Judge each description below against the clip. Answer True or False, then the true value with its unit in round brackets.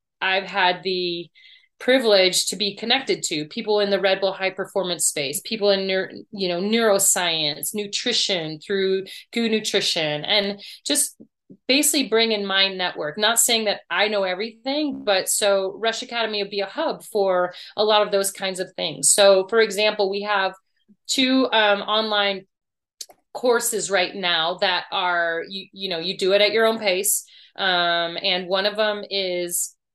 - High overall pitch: True (195 Hz)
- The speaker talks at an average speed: True (165 wpm)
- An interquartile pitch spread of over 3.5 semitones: False (2.5 semitones)